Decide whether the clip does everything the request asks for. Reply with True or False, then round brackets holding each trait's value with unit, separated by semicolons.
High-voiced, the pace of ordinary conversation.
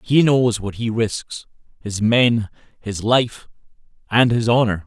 False (115 Hz; 150 wpm)